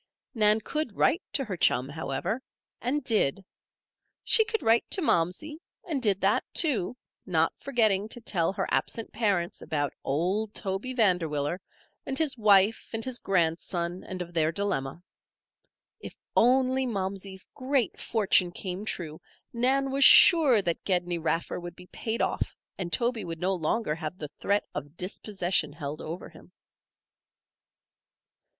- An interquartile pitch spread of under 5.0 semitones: No, wide, 5.5 semitones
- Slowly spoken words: No, average, 145 wpm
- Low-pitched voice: No, high, 195 Hz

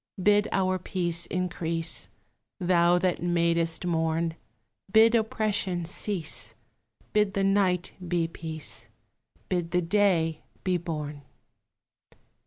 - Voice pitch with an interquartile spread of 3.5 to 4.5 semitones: No, average, 2.7 semitones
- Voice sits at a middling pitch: Yes, medium, 175 Hz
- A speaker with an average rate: No, slow, 100 wpm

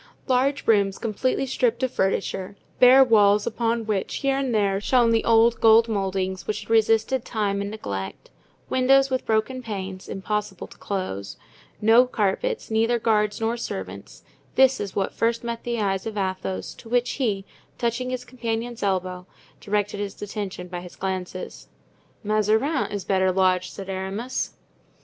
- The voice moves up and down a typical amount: Yes, average, 3.6 semitones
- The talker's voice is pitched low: No, high, 215 Hz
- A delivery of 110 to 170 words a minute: Yes, average, 155 wpm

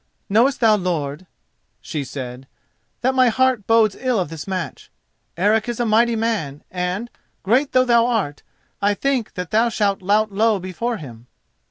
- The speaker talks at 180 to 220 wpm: No, average, 165 wpm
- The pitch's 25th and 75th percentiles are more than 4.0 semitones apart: Yes, average, 4.7 semitones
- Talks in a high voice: Yes, high, 215 Hz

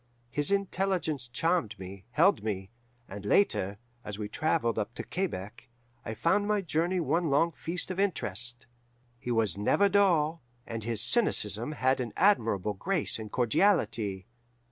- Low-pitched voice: Yes, low, 130 Hz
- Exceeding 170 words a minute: No, average, 145 wpm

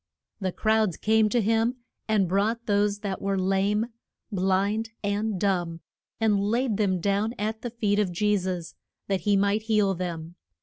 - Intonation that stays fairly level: Yes, narrow, 2.3 semitones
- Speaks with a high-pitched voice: Yes, high, 205 Hz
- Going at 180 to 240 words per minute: No, average, 165 wpm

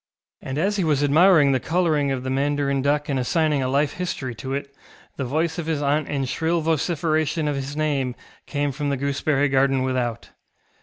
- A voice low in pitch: No, medium, 145 Hz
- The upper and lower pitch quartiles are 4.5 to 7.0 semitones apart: No, narrow, 2.5 semitones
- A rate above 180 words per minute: Yes, average, 195 wpm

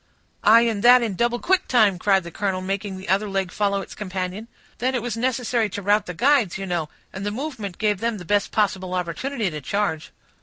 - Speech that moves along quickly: Yes, fast, 220 wpm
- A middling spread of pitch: Yes, average, 3.6 semitones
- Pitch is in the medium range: No, high, 205 Hz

